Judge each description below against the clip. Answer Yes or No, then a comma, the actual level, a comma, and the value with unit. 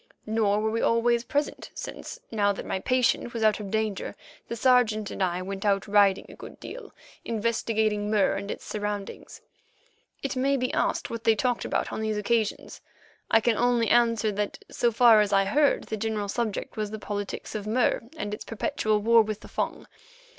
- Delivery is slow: No, average, 190 wpm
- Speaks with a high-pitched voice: Yes, high, 220 Hz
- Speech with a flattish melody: Yes, narrow, 2.2 semitones